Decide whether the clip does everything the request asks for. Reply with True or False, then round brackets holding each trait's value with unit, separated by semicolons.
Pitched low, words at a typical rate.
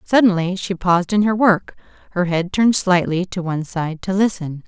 False (185 Hz; 190 wpm)